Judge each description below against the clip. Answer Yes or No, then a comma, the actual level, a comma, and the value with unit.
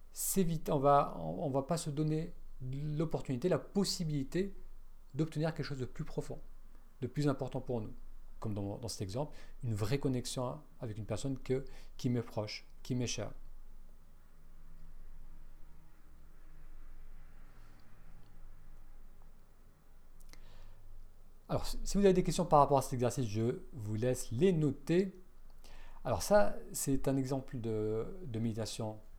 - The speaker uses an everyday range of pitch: No, wide, 6.7 semitones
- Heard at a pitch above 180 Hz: No, low, 125 Hz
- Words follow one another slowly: Yes, slow, 135 wpm